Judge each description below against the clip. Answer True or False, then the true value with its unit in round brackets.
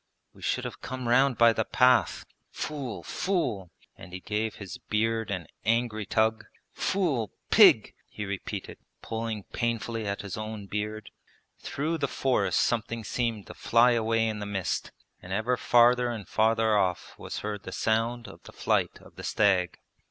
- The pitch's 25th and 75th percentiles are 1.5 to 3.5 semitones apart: True (2.4 semitones)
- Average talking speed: True (165 wpm)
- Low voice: True (110 Hz)